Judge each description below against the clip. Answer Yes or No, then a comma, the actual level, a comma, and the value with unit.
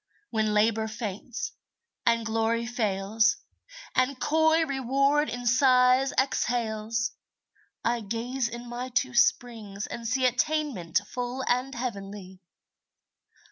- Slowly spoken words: Yes, slow, 105 wpm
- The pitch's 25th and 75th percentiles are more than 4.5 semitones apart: No, average, 2.8 semitones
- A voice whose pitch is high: Yes, high, 240 Hz